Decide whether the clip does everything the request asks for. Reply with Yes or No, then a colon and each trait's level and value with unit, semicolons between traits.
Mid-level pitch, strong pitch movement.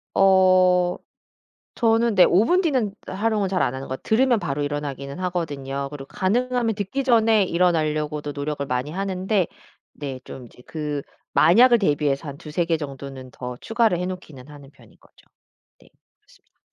Yes: medium, 175 Hz; wide, 6.3 semitones